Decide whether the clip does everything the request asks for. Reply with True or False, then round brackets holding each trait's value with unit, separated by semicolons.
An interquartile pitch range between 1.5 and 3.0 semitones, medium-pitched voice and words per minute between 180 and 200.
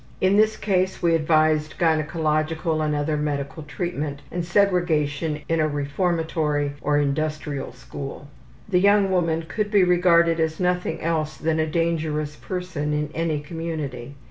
False (2.6 semitones; 160 Hz; 145 wpm)